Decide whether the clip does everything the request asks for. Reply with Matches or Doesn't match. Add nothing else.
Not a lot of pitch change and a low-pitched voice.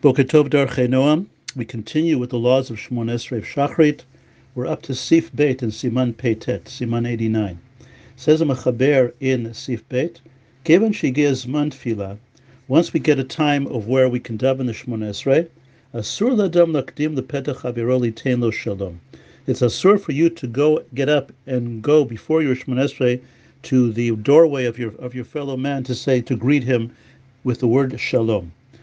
Doesn't match